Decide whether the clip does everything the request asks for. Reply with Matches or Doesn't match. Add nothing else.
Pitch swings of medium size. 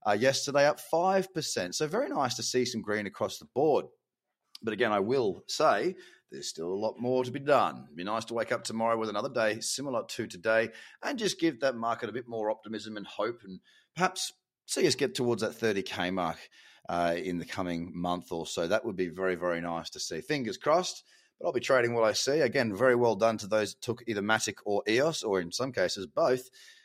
Matches